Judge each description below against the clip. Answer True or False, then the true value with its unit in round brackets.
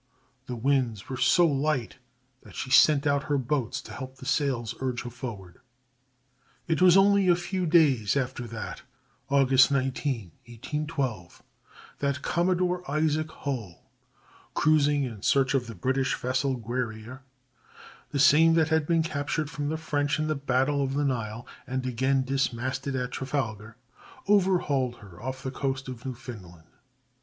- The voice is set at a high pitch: False (135 Hz)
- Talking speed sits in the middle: True (150 wpm)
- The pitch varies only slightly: False (3.5 semitones)